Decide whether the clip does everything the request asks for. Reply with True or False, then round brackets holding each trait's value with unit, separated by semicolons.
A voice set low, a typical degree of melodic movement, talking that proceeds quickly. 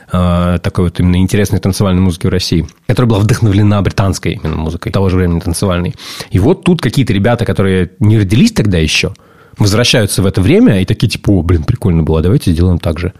True (95 Hz; 3.6 semitones; 195 wpm)